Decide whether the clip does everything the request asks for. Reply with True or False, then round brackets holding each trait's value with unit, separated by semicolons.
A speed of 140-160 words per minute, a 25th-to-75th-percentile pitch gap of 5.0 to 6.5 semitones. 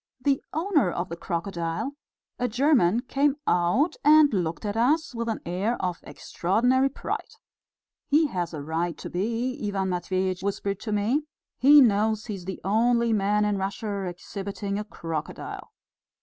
True (155 wpm; 5.3 semitones)